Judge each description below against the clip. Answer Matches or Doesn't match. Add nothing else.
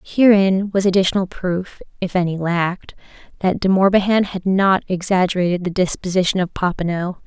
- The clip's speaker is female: Matches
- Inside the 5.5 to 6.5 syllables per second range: Doesn't match